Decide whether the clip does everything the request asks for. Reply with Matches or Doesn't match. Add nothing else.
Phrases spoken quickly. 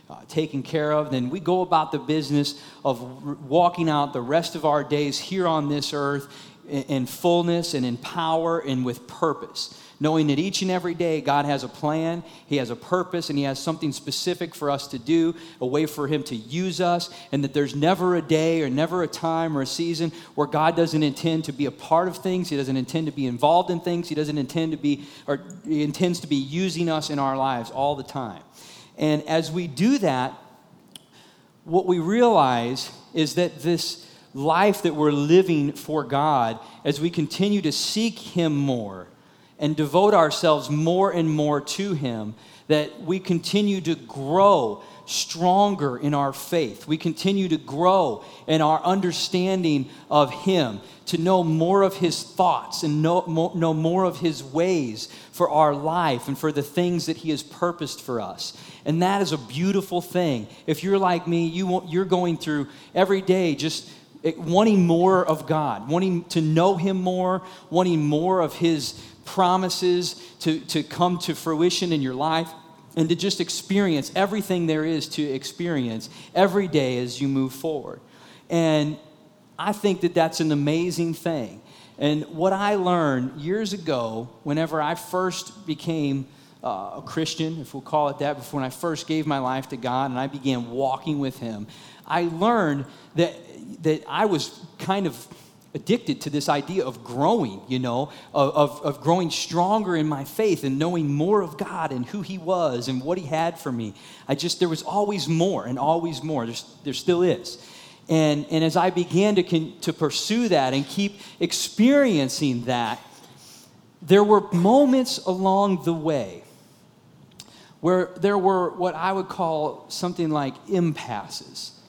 Doesn't match